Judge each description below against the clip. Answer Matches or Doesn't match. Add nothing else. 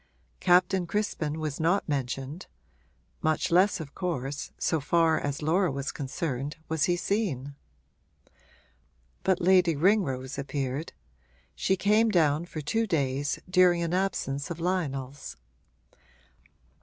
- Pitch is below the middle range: Doesn't match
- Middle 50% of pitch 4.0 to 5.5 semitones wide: Matches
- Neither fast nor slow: Doesn't match